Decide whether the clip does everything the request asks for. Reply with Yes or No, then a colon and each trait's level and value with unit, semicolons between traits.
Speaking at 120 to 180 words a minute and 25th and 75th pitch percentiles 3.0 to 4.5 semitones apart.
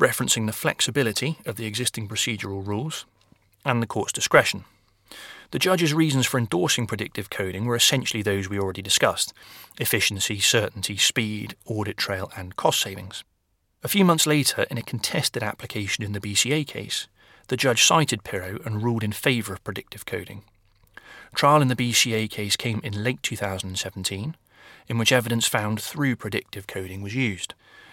Yes: average, 160 wpm; average, 3.7 semitones